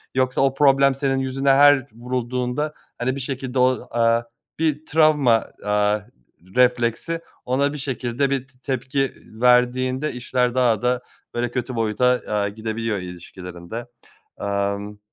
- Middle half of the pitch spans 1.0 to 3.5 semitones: Yes, average, 2.9 semitones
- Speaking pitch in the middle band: No, low, 125 Hz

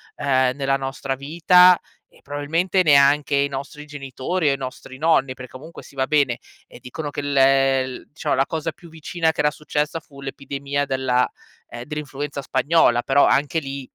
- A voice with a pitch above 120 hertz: Yes, medium, 140 Hz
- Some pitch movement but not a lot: No, narrow, 2.1 semitones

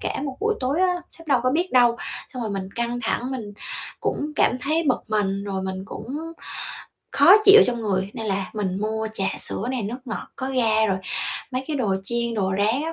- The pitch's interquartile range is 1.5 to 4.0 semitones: No, average, 4.4 semitones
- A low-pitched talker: No, high, 235 Hz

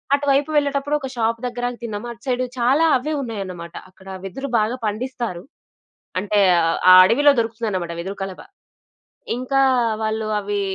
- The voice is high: Yes, high, 230 Hz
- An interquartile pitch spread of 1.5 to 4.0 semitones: No, average, 4.4 semitones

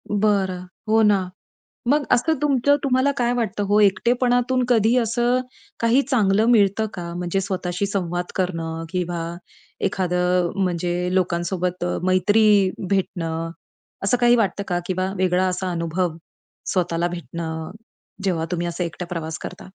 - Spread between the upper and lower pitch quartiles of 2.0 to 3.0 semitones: No, average, 3.7 semitones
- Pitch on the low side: No, medium, 185 Hz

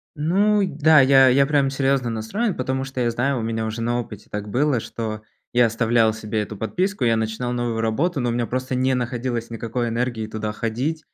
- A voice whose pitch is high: No, low, 120 Hz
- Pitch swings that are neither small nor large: Yes, average, 3.2 semitones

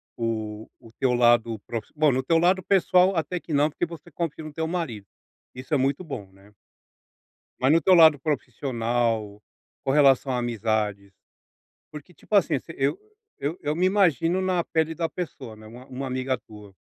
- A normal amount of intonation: No, wide, 6.2 semitones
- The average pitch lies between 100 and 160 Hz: Yes, low, 135 Hz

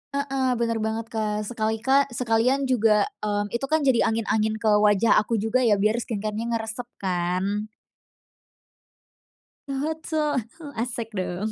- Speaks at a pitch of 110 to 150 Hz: No, high, 225 Hz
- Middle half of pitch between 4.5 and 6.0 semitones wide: No, average, 2.9 semitones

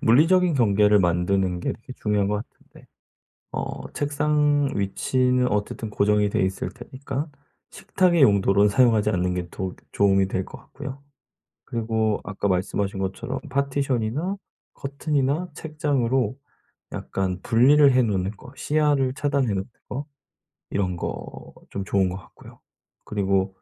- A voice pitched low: Yes, low, 110 Hz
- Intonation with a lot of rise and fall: Yes, wide, 6.1 semitones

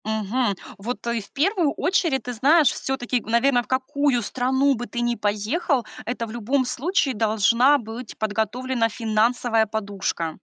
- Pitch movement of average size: Yes, average, 3.4 semitones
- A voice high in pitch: Yes, high, 240 Hz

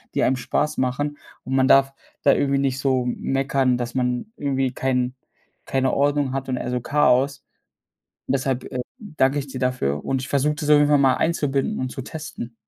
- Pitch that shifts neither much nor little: No, narrow, 1.9 semitones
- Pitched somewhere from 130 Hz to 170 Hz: Yes, low, 135 Hz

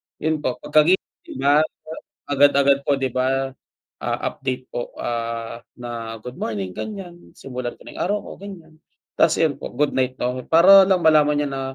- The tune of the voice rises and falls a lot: No, average, 4.1 semitones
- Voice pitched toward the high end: No, medium, 140 Hz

